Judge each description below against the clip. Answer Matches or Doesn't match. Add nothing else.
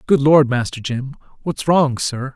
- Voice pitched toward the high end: Doesn't match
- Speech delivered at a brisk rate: Doesn't match